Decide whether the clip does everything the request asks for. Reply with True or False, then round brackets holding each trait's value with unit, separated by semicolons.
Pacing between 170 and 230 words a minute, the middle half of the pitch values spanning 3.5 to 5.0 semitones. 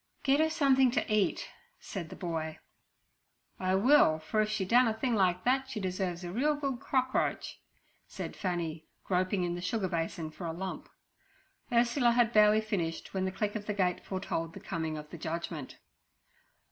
False (180 wpm; 5.5 semitones)